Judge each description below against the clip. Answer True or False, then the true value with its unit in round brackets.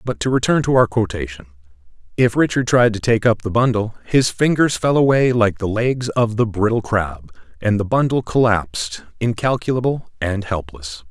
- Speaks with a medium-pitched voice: False (110 Hz)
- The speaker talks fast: False (175 wpm)